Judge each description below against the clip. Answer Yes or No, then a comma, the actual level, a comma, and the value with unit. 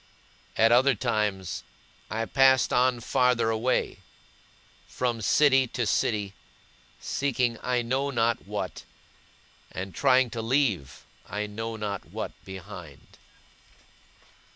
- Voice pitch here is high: No, low, 115 Hz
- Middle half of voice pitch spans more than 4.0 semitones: No, average, 3.4 semitones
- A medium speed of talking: No, slow, 105 wpm